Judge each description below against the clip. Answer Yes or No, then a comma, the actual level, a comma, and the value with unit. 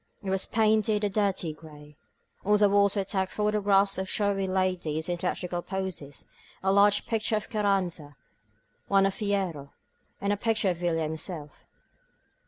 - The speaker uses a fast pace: No, average, 160 wpm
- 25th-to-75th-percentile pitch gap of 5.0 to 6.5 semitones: No, average, 2.9 semitones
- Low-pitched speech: No, high, 195 Hz